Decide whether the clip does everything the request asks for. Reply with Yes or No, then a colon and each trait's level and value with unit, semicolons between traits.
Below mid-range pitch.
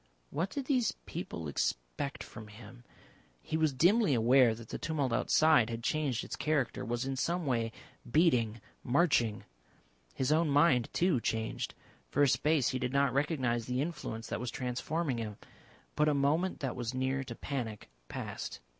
Yes: low, 130 Hz